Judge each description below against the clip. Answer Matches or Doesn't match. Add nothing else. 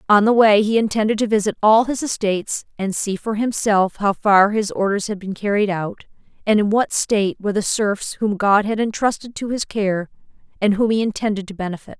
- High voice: Matches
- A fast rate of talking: Matches